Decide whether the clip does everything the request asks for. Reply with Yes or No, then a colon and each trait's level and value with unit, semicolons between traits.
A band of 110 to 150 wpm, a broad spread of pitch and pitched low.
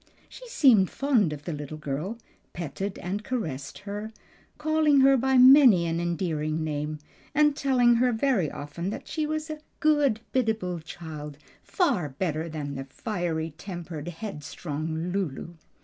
No: average, 140 wpm; wide, 8.6 semitones; medium, 180 Hz